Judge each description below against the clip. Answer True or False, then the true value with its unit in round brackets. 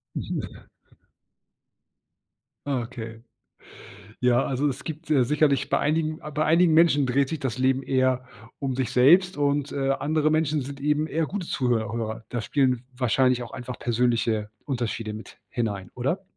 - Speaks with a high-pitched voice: False (130 Hz)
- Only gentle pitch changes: False (3.6 semitones)